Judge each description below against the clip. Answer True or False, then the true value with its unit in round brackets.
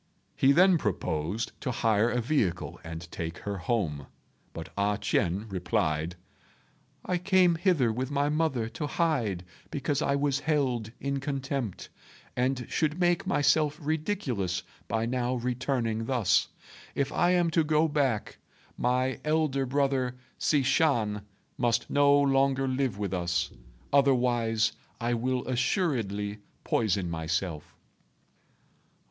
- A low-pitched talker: True (125 Hz)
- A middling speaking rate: False (125 wpm)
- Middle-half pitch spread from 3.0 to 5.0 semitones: False (5.6 semitones)